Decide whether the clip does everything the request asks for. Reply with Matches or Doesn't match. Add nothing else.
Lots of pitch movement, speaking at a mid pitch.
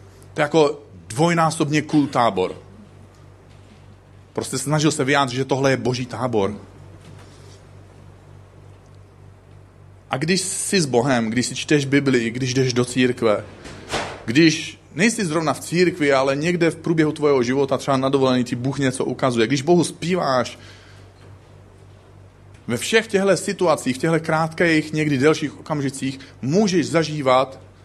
Doesn't match